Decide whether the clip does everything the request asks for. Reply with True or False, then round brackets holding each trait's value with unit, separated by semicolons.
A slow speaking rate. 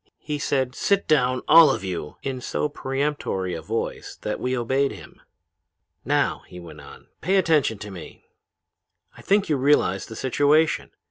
False (160 wpm)